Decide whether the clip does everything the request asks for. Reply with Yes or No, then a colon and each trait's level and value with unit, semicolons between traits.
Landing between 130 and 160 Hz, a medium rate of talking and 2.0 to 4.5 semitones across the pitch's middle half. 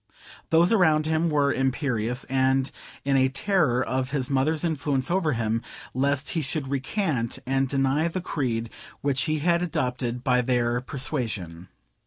Yes: low, 135 Hz; average, 150 wpm; average, 3.6 semitones